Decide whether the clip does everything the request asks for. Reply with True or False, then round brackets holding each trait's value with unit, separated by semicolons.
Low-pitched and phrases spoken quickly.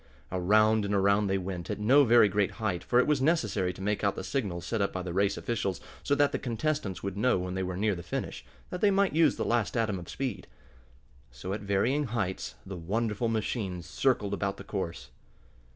True (100 Hz; 215 wpm)